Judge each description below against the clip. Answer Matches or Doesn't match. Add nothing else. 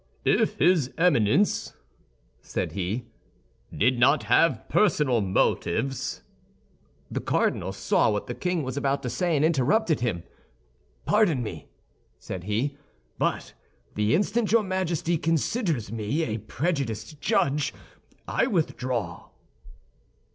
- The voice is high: Doesn't match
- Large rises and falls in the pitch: Matches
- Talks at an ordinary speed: Doesn't match